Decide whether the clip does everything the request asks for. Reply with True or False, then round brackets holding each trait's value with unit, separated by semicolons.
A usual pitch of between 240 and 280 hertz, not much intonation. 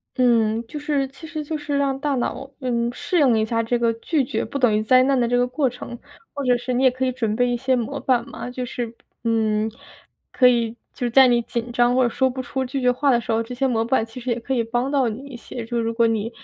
True (245 Hz; 2.2 semitones)